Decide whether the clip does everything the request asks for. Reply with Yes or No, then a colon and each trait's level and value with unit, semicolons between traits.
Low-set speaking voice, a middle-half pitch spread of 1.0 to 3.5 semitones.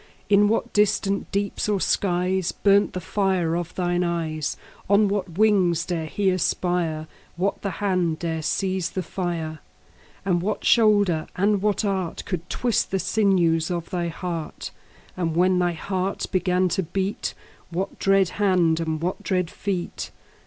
No: medium, 185 Hz; narrow, 2.6 semitones